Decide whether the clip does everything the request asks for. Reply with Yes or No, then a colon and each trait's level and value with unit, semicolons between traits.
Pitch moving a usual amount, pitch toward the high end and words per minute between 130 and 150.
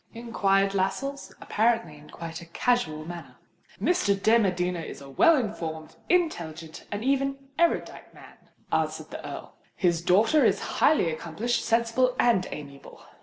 No: wide, 6.4 semitones; high, 195 Hz; average, 140 wpm